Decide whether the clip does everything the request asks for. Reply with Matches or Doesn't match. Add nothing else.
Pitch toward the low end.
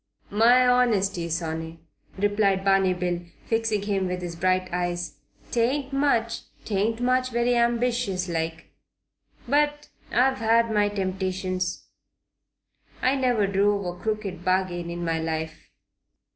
Doesn't match